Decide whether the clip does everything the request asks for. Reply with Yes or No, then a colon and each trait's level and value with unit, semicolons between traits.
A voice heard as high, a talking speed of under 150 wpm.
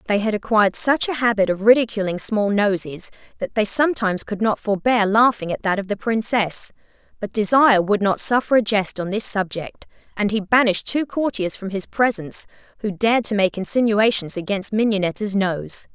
No: high, 210 Hz; average, 180 wpm